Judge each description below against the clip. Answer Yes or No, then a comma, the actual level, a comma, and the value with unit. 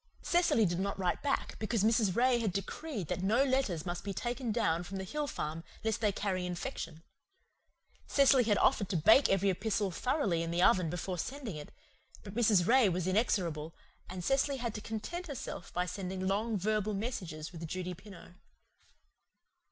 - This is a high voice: Yes, high, 200 Hz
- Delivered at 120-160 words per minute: No, average, 175 wpm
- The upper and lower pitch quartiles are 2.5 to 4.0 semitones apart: No, average, 4.8 semitones